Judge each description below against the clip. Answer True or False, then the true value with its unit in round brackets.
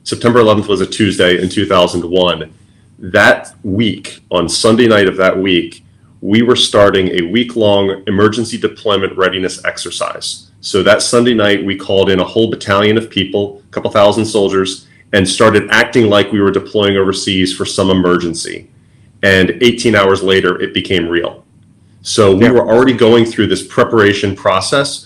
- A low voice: True (100 Hz)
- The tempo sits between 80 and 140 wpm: False (165 wpm)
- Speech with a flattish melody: False (3.0 semitones)